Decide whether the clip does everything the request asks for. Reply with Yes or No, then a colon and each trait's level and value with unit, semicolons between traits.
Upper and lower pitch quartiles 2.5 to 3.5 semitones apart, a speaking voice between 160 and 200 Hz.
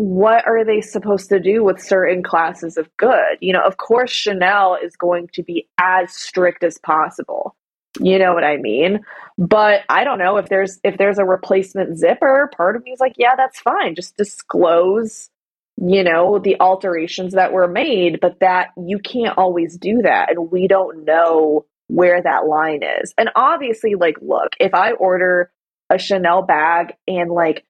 Yes: average, 2.8 semitones; medium, 185 Hz